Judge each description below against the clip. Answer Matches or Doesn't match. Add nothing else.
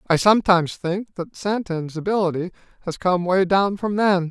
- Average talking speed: Matches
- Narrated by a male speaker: Matches